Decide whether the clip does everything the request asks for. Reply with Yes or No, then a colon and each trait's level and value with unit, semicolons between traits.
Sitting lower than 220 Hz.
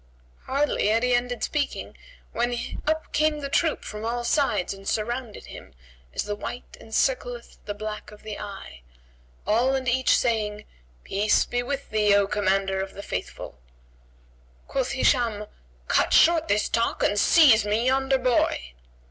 No: high, 235 Hz